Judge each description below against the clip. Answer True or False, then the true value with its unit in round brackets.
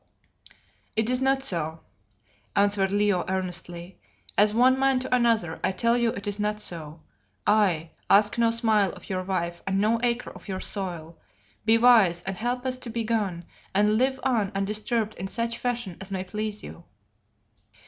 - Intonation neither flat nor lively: True (3.8 semitones)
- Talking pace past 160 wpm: True (170 wpm)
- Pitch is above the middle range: True (210 Hz)